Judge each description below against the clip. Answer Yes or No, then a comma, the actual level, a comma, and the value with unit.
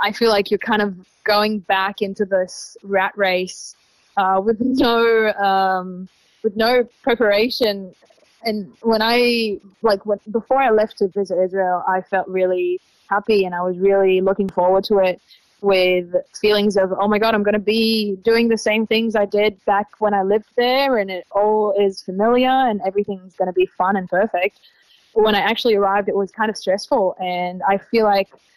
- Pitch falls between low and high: No, high, 205 Hz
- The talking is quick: Yes, fast, 190 wpm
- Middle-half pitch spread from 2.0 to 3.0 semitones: Yes, narrow, 2.5 semitones